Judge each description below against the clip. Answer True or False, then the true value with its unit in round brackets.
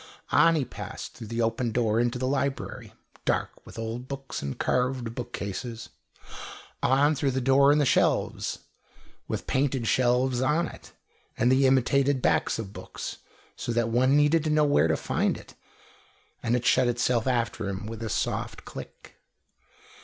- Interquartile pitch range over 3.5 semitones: False (2.9 semitones)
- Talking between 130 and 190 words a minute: True (165 wpm)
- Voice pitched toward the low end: True (125 Hz)